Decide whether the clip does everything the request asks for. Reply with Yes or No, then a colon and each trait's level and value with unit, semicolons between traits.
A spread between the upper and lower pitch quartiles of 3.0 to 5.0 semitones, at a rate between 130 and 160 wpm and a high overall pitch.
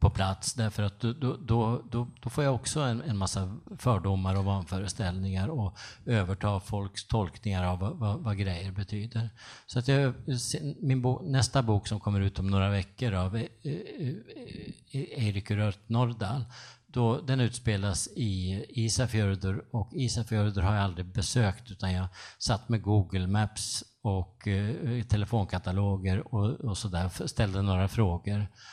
No: average, 3.5 semitones; average, 155 wpm; low, 105 Hz